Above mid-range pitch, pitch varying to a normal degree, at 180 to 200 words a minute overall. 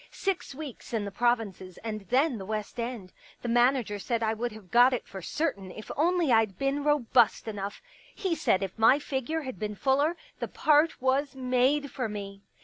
Yes: high, 245 Hz; average, 5.0 semitones; average, 195 wpm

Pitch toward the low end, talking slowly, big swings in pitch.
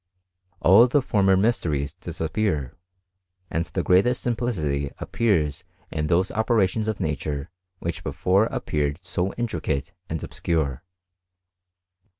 Yes: very low, 90 Hz; slow, 110 wpm; wide, 5.9 semitones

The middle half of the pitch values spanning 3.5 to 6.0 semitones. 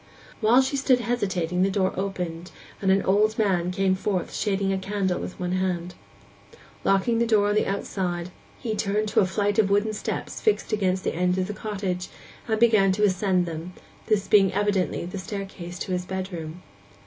No: narrow, 2.4 semitones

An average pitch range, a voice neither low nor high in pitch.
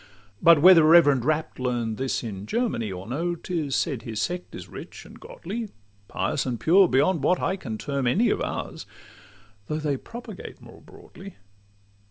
No: wide, 6.3 semitones; medium, 150 Hz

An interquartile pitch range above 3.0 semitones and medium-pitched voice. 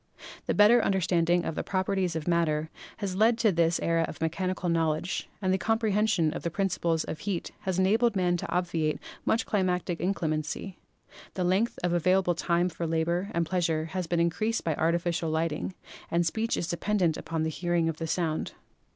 No: narrow, 2.6 semitones; medium, 175 Hz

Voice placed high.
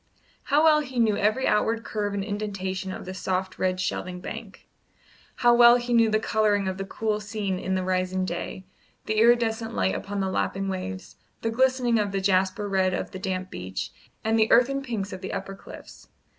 Yes: high, 200 Hz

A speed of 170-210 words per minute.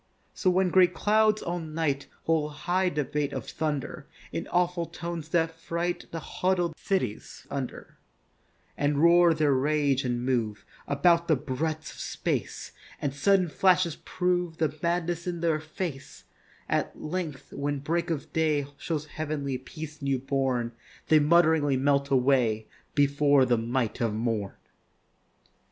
No: average, 140 wpm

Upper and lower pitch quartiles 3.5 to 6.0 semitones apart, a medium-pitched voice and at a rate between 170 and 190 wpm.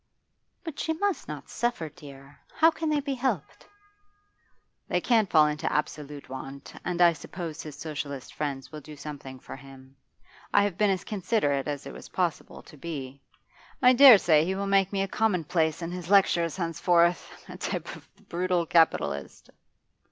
Yes: average, 5.2 semitones; medium, 170 Hz; average, 175 wpm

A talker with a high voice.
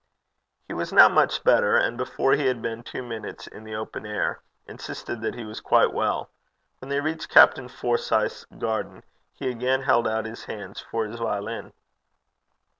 No: low, 115 Hz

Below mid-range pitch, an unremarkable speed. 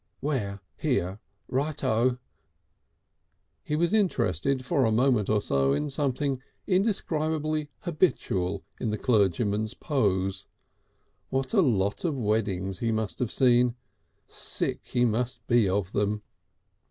No: low, 120 Hz; slow, 125 wpm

